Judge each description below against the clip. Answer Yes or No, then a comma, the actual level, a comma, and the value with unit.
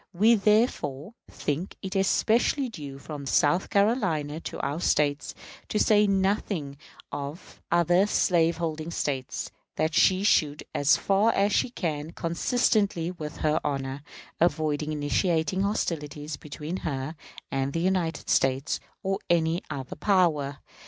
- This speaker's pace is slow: Yes, slow, 125 wpm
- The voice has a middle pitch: Yes, medium, 165 Hz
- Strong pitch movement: No, average, 4.7 semitones